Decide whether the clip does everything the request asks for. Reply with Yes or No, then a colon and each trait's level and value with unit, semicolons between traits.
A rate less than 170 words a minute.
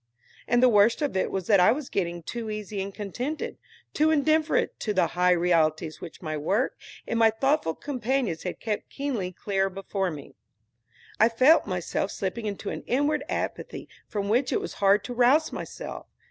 No: average, 180 wpm